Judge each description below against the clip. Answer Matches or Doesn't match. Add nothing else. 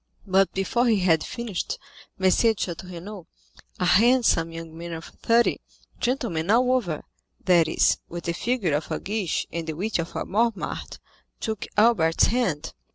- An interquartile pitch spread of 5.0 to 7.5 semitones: Matches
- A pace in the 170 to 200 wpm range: Doesn't match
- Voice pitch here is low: Doesn't match